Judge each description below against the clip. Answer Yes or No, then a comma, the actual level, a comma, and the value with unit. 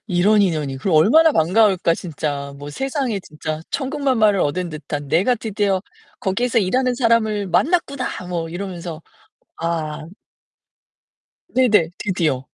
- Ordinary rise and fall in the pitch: No, wide, 6.4 semitones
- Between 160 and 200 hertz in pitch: Yes, high, 190 Hz